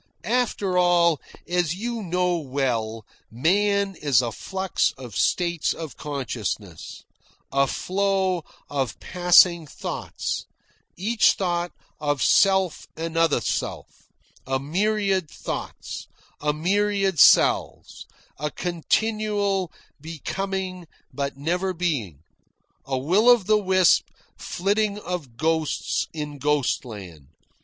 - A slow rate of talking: Yes, slow, 100 wpm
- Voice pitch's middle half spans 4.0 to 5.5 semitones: Yes, average, 5.2 semitones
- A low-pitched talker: No, medium, 175 Hz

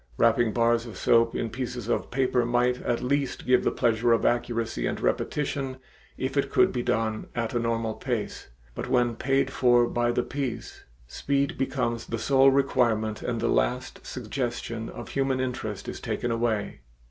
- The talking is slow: No, average, 170 wpm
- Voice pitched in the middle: No, low, 120 Hz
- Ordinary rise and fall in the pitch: No, narrow, 2.1 semitones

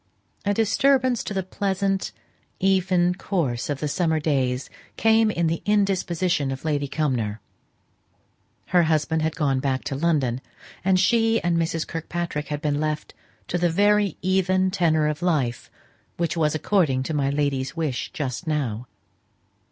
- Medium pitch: Yes, medium, 165 Hz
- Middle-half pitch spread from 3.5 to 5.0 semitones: Yes, average, 4.5 semitones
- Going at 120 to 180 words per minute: Yes, average, 150 wpm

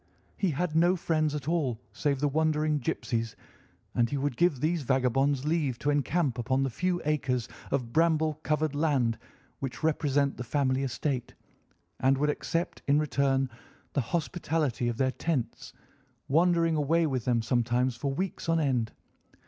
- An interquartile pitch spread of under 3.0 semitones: No, average, 3.5 semitones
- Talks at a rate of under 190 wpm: Yes, average, 155 wpm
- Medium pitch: Yes, medium, 145 Hz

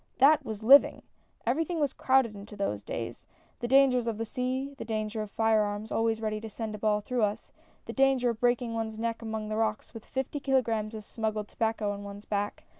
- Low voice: No, high, 225 Hz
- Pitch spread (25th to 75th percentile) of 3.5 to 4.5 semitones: No, average, 2.8 semitones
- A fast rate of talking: Yes, fast, 230 wpm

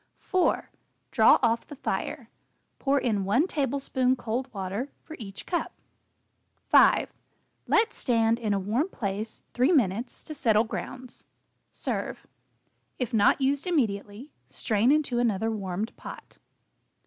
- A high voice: Yes, high, 240 Hz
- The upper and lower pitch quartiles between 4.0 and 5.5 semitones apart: Yes, average, 4.6 semitones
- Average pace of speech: No, slow, 125 wpm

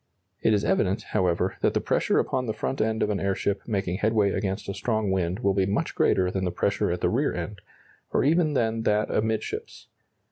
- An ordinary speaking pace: No, fast, 210 wpm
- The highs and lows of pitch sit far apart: No, narrow, 2.6 semitones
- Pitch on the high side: No, low, 100 Hz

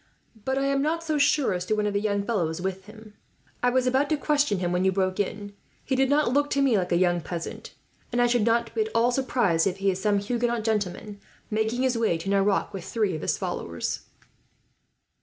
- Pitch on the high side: Yes, high, 215 Hz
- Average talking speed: No, fast, 230 wpm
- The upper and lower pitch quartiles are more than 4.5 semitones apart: Yes, average, 5.2 semitones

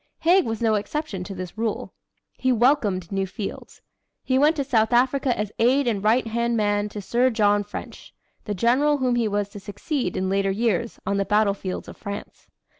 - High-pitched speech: Yes, high, 220 Hz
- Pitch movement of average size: Yes, average, 3.7 semitones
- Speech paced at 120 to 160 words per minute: No, average, 190 wpm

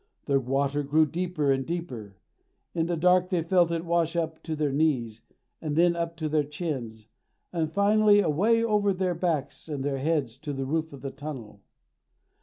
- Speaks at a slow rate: No, average, 185 wpm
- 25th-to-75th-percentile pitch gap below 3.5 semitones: No, average, 3.8 semitones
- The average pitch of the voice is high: No, medium, 160 Hz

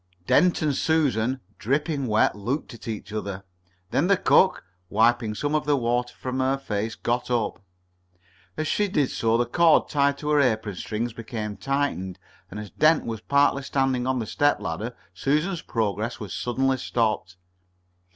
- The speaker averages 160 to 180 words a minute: Yes, average, 165 wpm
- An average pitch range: Yes, average, 4.5 semitones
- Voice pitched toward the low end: Yes, low, 125 Hz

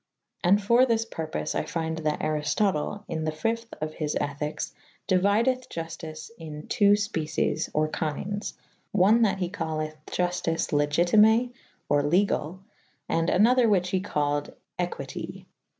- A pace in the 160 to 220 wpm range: No, slow, 135 wpm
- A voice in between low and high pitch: Yes, medium, 175 Hz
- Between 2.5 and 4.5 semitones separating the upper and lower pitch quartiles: No, average, 4.9 semitones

